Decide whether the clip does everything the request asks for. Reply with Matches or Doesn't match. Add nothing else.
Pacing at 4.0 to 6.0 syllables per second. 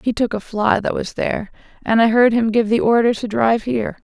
Matches